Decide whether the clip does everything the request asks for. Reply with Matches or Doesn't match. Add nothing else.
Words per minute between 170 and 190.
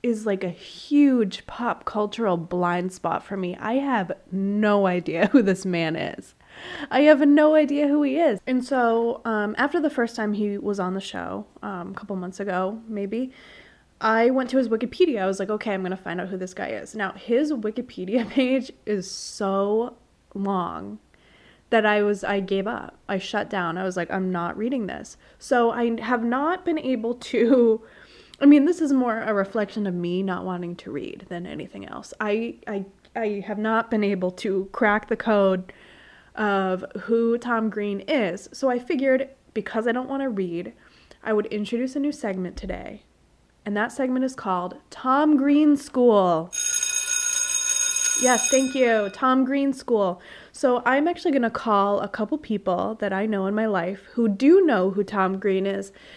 Matches